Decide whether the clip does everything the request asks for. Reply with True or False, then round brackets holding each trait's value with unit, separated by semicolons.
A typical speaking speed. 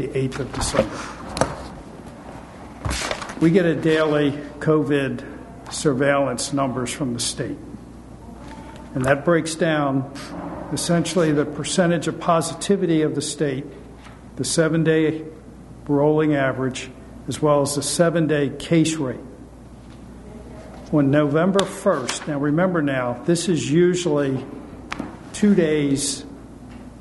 False (105 wpm)